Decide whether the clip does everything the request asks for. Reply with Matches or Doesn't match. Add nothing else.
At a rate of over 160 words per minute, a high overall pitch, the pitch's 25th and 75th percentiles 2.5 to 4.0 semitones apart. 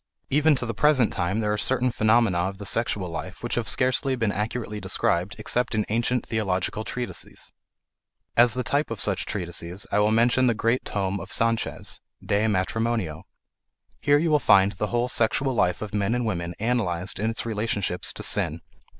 Doesn't match